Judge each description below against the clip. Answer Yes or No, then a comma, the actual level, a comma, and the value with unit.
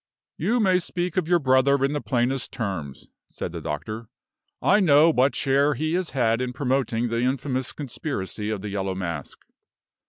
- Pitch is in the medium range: No, low, 130 Hz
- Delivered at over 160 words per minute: Yes, average, 175 wpm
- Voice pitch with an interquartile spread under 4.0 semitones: No, average, 4.9 semitones